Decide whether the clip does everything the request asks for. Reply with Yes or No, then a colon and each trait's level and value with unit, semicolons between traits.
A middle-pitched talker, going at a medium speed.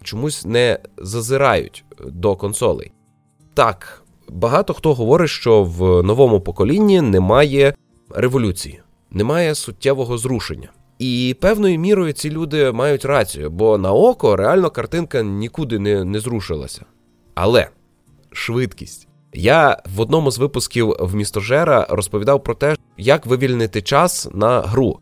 No: low, 125 Hz; average, 120 wpm